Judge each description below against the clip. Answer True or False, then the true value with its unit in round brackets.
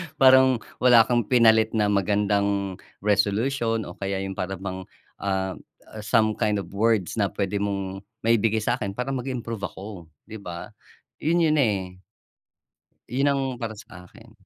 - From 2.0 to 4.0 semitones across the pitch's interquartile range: True (3.1 semitones)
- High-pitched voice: False (105 Hz)